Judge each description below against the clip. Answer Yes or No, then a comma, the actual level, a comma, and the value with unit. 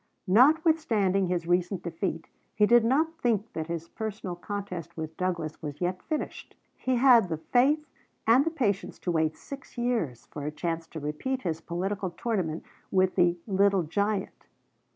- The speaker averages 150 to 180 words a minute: Yes, average, 160 wpm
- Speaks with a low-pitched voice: No, high, 190 Hz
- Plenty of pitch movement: Yes, wide, 5.9 semitones